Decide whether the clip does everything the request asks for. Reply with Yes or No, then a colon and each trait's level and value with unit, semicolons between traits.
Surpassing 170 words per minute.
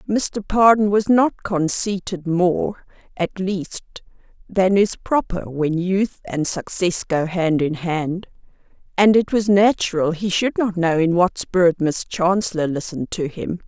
No: average, 155 wpm